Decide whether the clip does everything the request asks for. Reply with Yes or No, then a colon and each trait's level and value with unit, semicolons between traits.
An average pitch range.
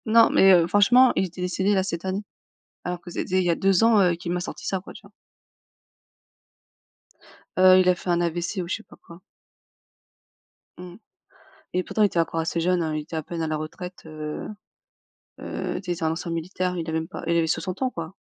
No: narrow, 2.1 semitones